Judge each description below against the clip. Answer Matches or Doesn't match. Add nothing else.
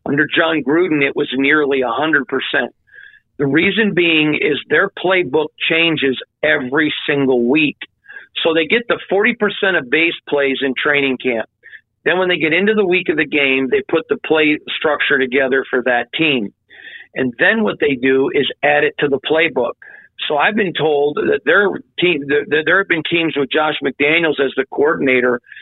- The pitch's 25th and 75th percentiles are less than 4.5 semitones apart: Doesn't match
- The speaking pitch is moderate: Matches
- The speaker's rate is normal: Matches